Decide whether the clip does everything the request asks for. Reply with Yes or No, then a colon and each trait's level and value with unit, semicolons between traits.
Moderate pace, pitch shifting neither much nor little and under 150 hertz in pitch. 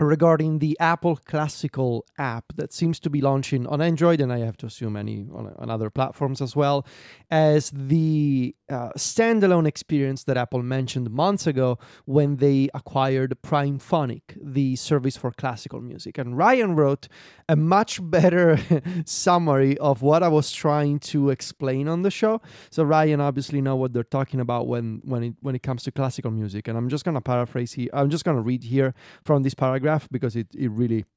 Yes: average, 185 wpm; average, 3.5 semitones; medium, 140 Hz